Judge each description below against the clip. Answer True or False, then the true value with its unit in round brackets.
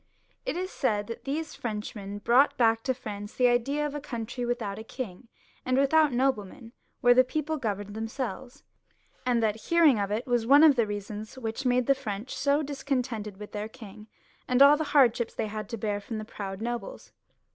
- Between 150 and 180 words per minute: False (200 wpm)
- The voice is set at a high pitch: True (240 Hz)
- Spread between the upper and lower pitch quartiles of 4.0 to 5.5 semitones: True (4.3 semitones)